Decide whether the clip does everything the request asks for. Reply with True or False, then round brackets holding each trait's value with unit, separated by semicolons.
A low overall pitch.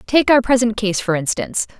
False (225 Hz)